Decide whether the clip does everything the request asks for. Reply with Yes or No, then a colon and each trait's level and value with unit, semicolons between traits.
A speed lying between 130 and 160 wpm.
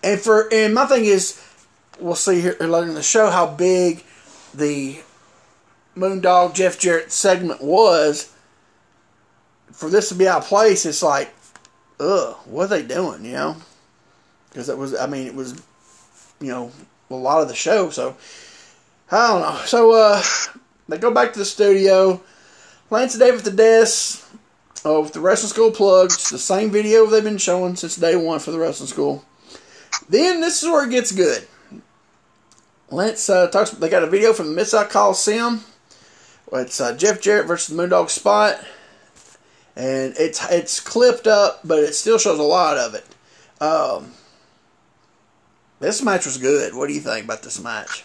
No: average, 175 wpm